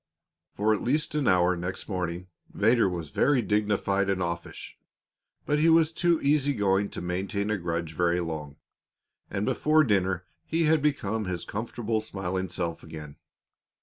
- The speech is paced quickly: No, average, 155 wpm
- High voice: No, low, 100 Hz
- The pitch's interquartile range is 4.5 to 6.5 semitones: Yes, wide, 5.4 semitones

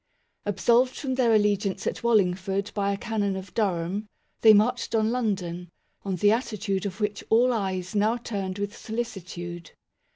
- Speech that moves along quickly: No, average, 160 wpm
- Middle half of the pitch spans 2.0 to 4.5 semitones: Yes, average, 2.9 semitones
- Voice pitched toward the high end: Yes, high, 205 Hz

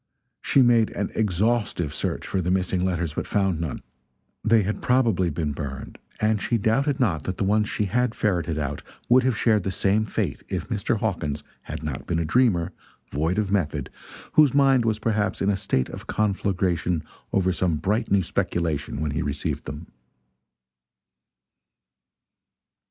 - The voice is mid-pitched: No, very low, 95 Hz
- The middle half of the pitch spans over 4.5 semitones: Yes, average, 5.0 semitones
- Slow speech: No, average, 165 wpm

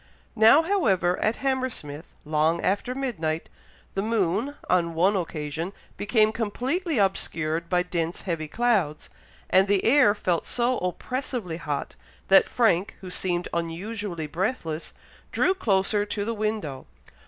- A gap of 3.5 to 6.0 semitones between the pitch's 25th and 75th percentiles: Yes, wide, 5.4 semitones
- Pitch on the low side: No, high, 195 Hz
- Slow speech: Yes, slow, 130 wpm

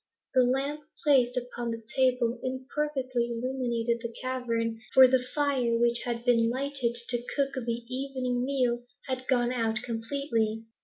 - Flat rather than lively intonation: Yes, narrow, 2.0 semitones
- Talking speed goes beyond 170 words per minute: No, average, 145 wpm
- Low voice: No, very high, 250 Hz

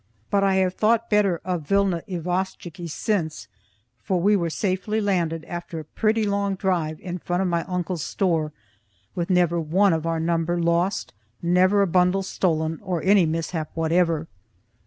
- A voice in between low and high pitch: Yes, medium, 180 Hz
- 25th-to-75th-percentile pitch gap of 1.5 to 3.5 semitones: Yes, narrow, 2.6 semitones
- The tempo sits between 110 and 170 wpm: Yes, average, 160 wpm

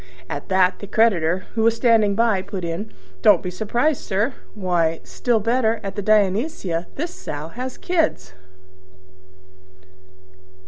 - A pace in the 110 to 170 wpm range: Yes, slow, 135 wpm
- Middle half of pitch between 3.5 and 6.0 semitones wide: Yes, average, 4.1 semitones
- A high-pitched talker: Yes, high, 205 Hz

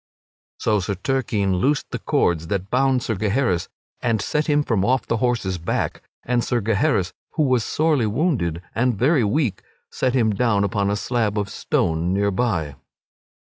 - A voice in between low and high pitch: No, low, 110 Hz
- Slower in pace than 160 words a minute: No, average, 170 wpm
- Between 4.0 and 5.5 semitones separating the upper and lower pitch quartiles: Yes, average, 4.6 semitones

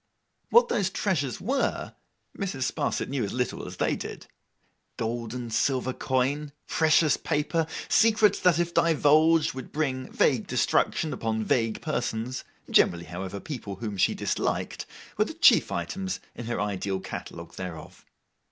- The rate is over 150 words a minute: No, average, 145 wpm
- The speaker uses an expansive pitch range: Yes, wide, 6.6 semitones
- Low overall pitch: Yes, low, 130 Hz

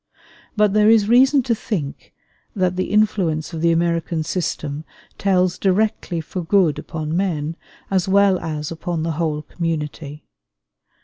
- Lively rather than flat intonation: No, average, 3.9 semitones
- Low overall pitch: No, medium, 175 Hz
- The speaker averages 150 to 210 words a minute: No, average, 140 wpm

